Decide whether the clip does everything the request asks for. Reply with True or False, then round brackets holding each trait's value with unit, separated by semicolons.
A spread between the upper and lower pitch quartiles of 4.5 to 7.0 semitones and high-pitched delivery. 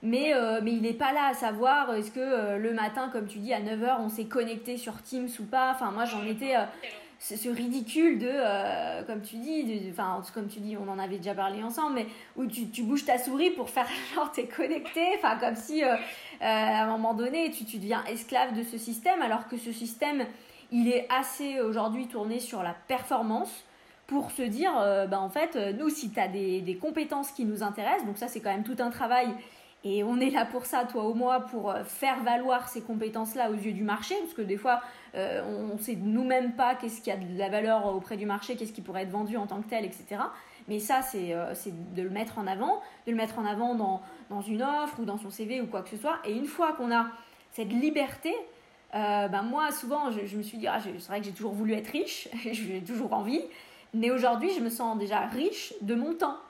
False (3.4 semitones; 230 Hz)